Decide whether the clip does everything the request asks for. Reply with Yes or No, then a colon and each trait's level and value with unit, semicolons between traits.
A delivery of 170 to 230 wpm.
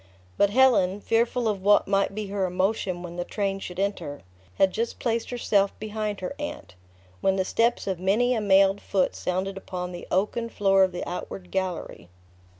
Yes: average, 180 wpm